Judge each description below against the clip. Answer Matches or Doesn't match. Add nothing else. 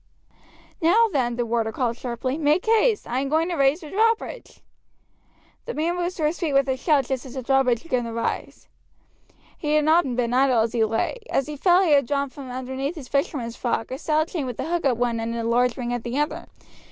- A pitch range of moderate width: Matches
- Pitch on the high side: Matches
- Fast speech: Matches